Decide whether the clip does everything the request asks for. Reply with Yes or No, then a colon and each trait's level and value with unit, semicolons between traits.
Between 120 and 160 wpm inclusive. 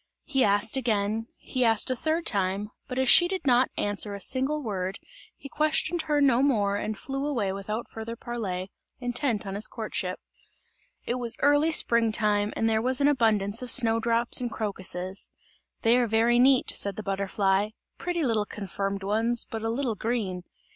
No: average, 180 wpm